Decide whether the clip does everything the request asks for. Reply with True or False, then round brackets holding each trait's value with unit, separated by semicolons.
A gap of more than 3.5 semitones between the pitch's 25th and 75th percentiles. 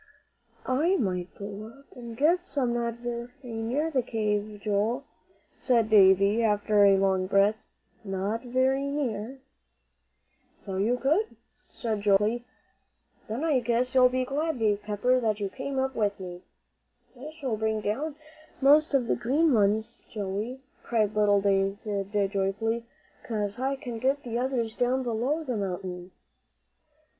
True (4.1 semitones)